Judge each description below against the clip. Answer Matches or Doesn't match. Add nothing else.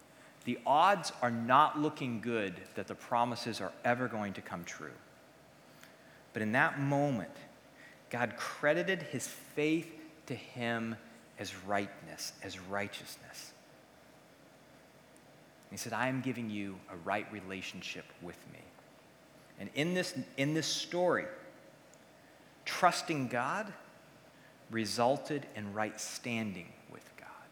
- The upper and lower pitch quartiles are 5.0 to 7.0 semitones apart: Matches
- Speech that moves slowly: Matches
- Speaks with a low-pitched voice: Matches